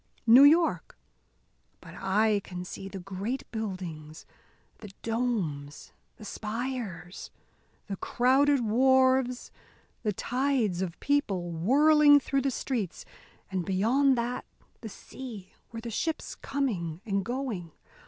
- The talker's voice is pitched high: Yes, high, 225 Hz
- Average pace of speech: No, slow, 115 wpm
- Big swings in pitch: Yes, wide, 5.7 semitones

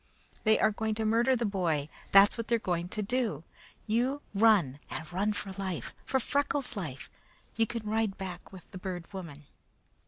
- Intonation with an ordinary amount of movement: Yes, average, 4.1 semitones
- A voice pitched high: Yes, high, 205 Hz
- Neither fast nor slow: Yes, average, 185 wpm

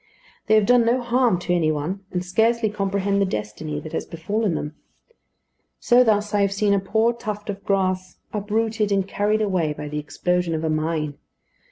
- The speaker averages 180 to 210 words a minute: Yes, average, 190 wpm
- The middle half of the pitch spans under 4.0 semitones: No, average, 4.5 semitones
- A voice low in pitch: No, high, 200 Hz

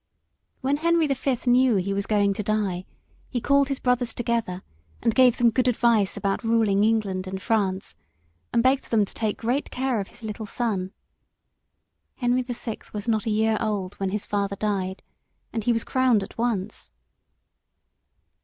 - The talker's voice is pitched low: No, high, 220 Hz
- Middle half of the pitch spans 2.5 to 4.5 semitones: Yes, average, 3.5 semitones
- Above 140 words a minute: Yes, average, 175 wpm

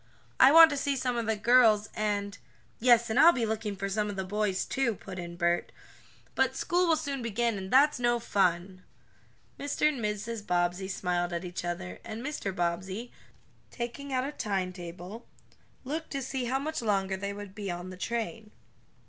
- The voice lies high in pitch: Yes, high, 215 Hz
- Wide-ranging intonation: No, average, 4.7 semitones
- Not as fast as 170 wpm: No, average, 190 wpm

